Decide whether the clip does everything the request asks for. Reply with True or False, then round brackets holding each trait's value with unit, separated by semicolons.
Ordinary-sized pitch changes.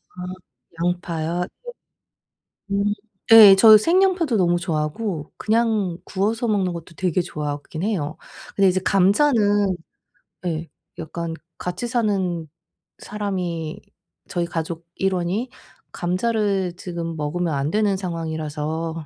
True (3.8 semitones)